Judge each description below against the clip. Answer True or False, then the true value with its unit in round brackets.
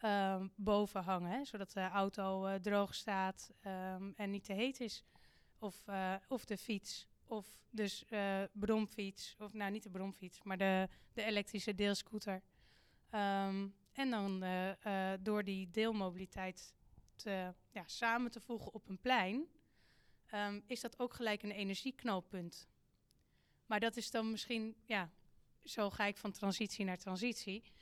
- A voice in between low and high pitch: False (205 Hz)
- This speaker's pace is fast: False (155 wpm)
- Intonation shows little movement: True (2.3 semitones)